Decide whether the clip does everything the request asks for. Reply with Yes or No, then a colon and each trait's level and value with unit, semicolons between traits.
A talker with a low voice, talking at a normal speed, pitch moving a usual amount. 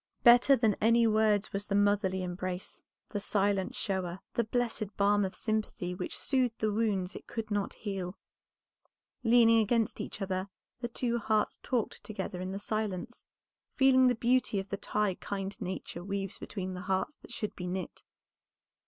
No: high, 205 Hz; average, 165 wpm; average, 3.1 semitones